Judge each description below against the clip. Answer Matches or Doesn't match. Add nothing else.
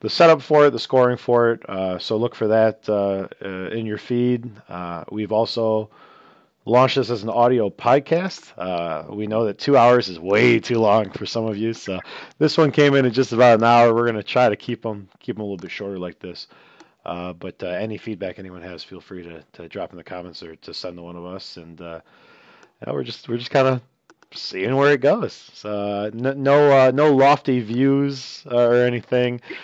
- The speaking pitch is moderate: Doesn't match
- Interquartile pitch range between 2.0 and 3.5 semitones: Doesn't match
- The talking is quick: Matches